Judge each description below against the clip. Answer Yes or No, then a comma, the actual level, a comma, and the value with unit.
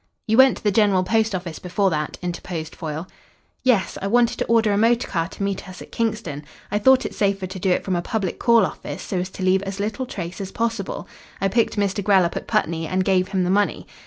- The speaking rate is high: Yes, fast, 245 wpm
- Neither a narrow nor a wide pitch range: Yes, average, 3.0 semitones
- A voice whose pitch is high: Yes, high, 195 Hz